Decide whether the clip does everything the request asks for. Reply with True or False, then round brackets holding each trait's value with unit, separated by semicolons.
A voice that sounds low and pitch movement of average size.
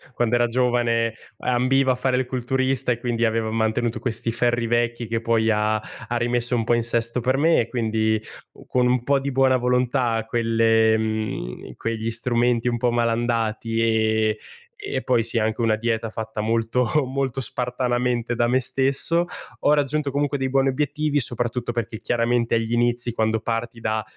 False (120 Hz; 1.8 semitones)